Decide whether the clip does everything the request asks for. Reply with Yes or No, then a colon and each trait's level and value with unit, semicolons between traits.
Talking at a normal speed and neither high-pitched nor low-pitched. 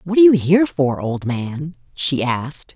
Yes: average, 195 wpm; medium, 155 Hz